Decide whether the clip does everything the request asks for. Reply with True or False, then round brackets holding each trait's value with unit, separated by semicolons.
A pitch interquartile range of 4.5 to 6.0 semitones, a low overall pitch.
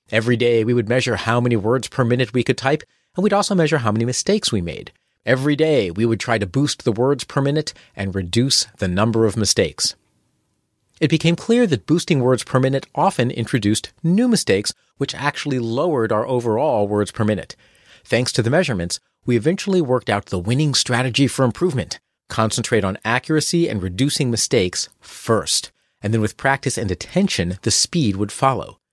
True (4.8 semitones; 125 Hz)